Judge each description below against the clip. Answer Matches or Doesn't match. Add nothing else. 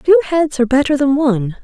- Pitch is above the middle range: Matches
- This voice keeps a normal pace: Doesn't match